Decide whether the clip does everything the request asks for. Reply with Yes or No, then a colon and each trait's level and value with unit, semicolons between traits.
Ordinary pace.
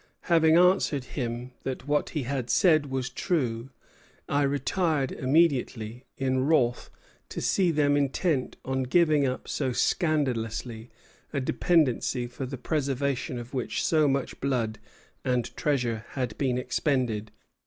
No: slow, 130 wpm